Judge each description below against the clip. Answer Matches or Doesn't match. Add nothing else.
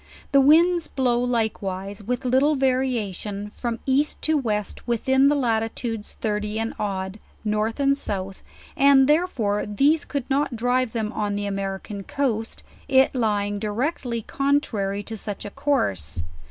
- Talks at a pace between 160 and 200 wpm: Doesn't match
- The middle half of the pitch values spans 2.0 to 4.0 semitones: Doesn't match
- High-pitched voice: Matches